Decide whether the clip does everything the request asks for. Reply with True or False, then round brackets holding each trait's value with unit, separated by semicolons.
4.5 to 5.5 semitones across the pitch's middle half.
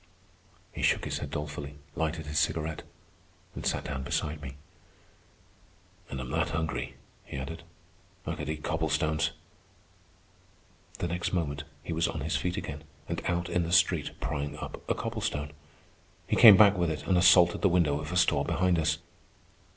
False (2.8 semitones)